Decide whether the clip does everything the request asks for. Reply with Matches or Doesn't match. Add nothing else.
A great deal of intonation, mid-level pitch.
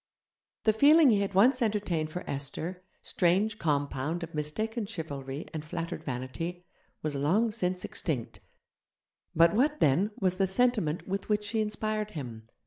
Matches